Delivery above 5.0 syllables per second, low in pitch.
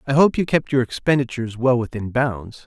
Yes: 5.6 syllables/s; low, 125 Hz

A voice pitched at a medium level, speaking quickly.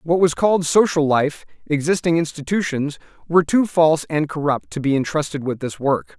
No: medium, 155 Hz; average, 175 wpm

